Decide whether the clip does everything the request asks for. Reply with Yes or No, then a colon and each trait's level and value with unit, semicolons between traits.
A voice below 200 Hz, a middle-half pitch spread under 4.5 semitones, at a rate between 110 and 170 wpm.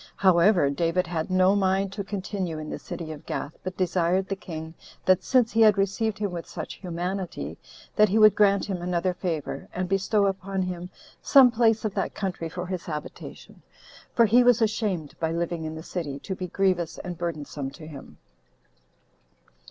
No: medium, 185 Hz; average, 2.9 semitones; average, 185 wpm